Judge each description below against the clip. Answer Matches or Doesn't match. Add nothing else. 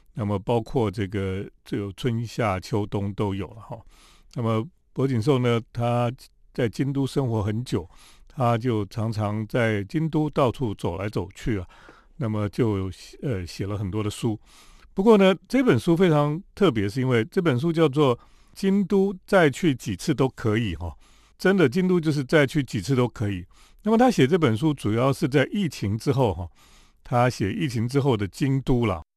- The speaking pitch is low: Matches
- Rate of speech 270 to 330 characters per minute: Doesn't match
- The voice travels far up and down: Matches